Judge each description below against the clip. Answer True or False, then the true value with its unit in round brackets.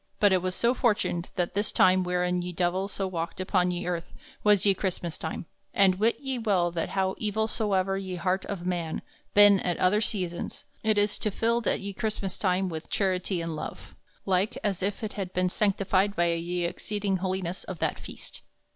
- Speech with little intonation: True (2.3 semitones)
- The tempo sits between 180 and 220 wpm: True (190 wpm)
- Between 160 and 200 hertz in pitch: True (190 Hz)